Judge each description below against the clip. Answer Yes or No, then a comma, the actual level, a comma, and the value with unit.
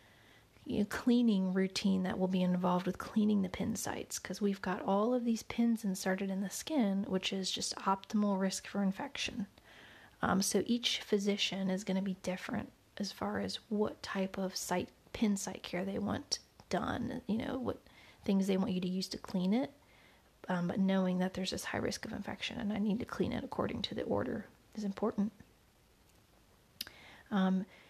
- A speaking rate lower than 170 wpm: No, average, 185 wpm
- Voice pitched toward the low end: No, high, 195 Hz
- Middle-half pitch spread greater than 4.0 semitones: No, narrow, 2.5 semitones